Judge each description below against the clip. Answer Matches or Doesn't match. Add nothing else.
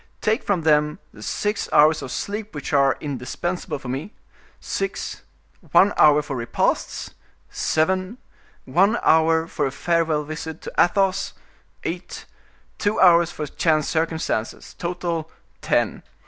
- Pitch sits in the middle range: Matches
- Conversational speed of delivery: Doesn't match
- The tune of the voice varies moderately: Matches